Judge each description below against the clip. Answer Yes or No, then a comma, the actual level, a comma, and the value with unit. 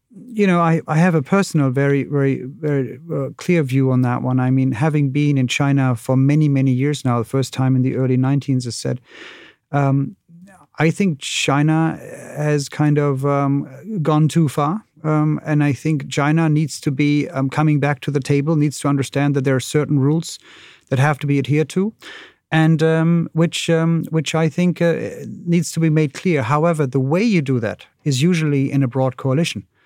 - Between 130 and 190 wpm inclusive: No, average, 200 wpm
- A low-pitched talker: No, medium, 145 Hz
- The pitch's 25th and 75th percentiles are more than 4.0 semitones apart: No, average, 3.0 semitones